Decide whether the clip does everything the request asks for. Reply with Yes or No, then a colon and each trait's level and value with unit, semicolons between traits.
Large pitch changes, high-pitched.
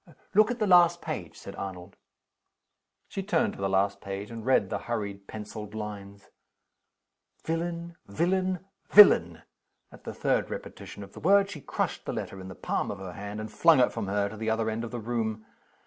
No: wide, 9.0 semitones; low, 110 Hz